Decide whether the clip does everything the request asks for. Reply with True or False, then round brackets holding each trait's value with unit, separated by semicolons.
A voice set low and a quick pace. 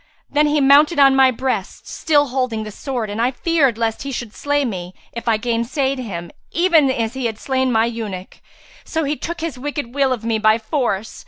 False (255 Hz; 210 wpm)